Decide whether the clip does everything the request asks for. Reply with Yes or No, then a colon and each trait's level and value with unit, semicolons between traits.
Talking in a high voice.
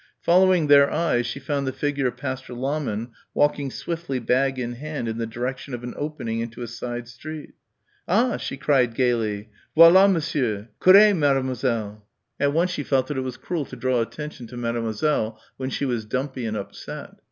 No: low, 130 Hz